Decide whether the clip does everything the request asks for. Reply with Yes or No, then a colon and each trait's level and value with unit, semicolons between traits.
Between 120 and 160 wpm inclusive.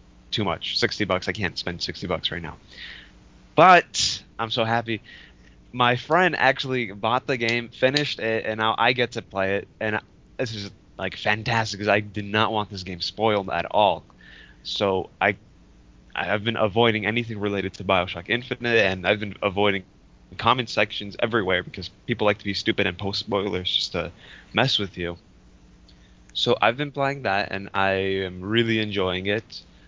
No: average, 175 wpm